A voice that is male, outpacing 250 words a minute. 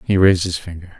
No: male; fast, 240 wpm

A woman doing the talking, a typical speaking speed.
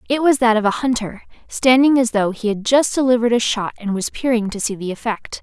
No: female; fast, 245 wpm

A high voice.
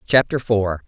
No: low, 110 Hz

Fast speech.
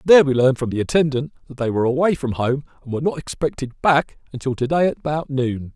Yes: fast, 230 wpm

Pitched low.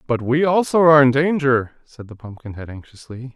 Yes: low, 130 Hz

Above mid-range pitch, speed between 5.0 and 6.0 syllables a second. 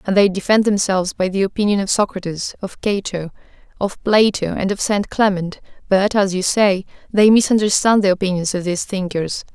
Yes: high, 195 Hz; 5.4 syllables/s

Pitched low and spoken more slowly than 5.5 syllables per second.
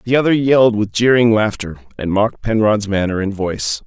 No: low, 105 Hz; 5.6 syllables/s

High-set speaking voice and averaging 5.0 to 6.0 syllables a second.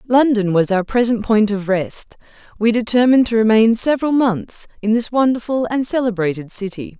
Yes: high, 225 Hz; 5.2 syllables/s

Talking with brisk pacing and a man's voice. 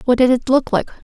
No: fast, 270 wpm; female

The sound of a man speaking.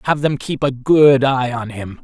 Yes: male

